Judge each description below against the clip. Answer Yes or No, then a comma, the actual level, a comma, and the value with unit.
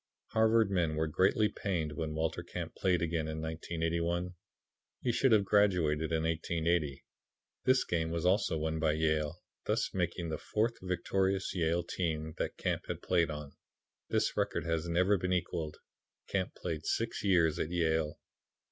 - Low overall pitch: Yes, very low, 85 Hz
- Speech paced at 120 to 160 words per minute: Yes, average, 155 wpm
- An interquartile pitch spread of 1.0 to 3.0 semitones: Yes, narrow, 2.6 semitones